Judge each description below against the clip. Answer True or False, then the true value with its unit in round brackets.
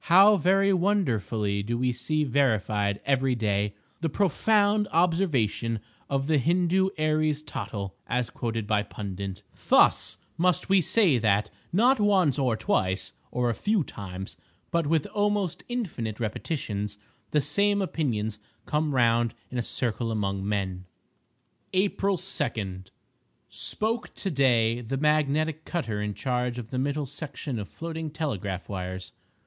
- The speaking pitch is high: False (135 Hz)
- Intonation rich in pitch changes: True (7.8 semitones)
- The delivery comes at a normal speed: False (130 wpm)